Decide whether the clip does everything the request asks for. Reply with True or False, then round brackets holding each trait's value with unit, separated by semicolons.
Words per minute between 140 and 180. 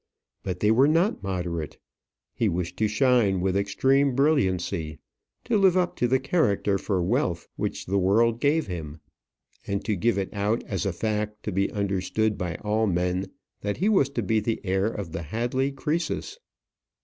True (175 wpm)